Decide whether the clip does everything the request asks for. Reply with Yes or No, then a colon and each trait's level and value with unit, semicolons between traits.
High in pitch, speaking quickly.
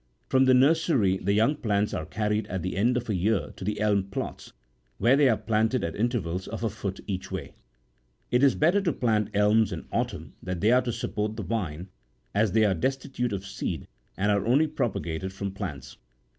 No: low, 105 Hz; fast, 210 wpm